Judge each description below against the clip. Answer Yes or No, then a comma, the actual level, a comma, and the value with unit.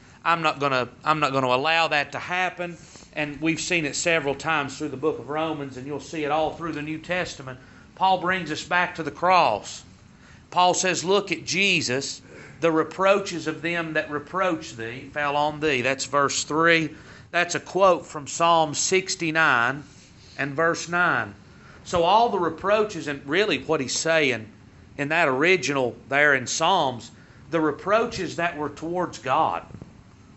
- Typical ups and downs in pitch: Yes, average, 3.6 semitones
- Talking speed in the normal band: Yes, average, 165 wpm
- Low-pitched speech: No, medium, 155 Hz